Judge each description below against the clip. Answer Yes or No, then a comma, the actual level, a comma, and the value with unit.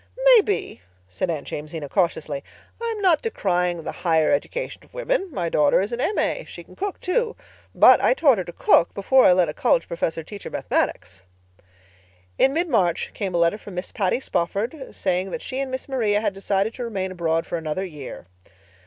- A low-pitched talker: No, high, 195 Hz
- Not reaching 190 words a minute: No, average, 195 wpm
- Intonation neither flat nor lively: No, wide, 7.7 semitones